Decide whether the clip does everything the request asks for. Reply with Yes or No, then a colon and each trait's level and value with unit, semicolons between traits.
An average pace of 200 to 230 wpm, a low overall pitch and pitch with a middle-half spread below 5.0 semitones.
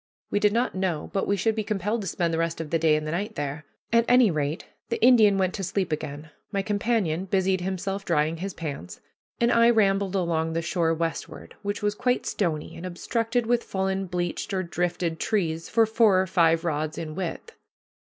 No: fast, 205 wpm; medium, 185 Hz; average, 4.1 semitones